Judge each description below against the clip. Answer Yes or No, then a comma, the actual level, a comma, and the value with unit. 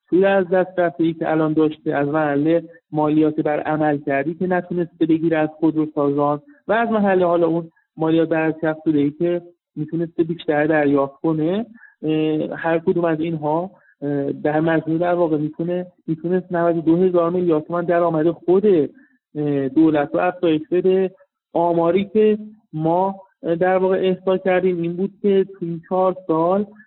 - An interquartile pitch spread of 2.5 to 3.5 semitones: Yes, average, 2.8 semitones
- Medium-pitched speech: Yes, medium, 170 Hz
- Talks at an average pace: Yes, average, 145 wpm